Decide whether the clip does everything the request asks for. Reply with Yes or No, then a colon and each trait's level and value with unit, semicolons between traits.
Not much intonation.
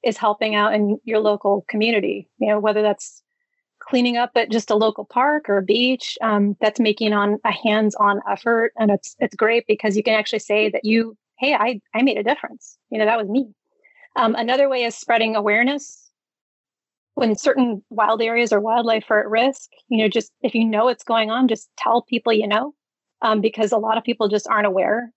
Yes: narrow, 2.0 semitones